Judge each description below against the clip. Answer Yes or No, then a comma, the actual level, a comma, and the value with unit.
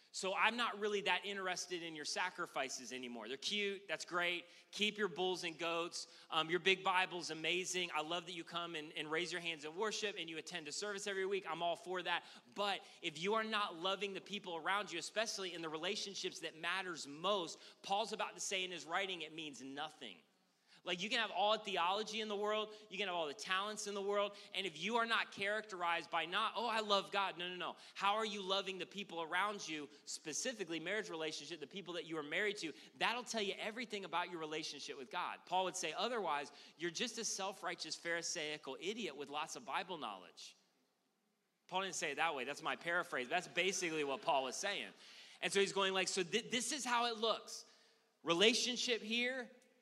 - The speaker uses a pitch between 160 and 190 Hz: Yes, medium, 185 Hz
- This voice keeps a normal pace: No, fast, 215 wpm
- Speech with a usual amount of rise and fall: Yes, average, 3.7 semitones